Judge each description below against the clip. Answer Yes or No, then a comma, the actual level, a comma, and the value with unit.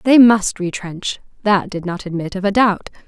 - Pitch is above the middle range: Yes, high, 195 Hz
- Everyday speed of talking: Yes, average, 195 wpm